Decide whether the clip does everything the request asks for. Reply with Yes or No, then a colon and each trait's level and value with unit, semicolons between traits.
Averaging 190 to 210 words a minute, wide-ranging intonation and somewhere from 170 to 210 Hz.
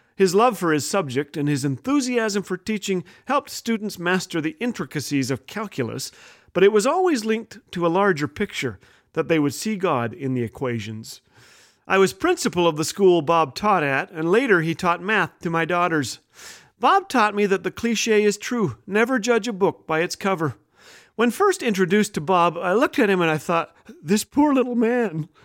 Yes: average, 195 wpm; wide, 5.8 semitones; high, 190 Hz